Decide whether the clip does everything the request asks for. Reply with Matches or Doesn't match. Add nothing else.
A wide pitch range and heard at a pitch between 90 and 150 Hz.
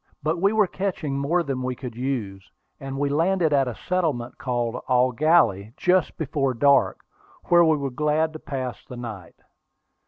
Doesn't match